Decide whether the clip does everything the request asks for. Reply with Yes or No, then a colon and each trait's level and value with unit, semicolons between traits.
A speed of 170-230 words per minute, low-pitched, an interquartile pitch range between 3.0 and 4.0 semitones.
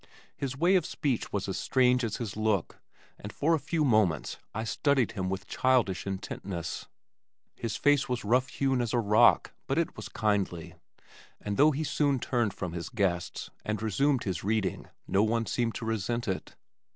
No: average, 180 wpm; low, 110 Hz; average, 4.7 semitones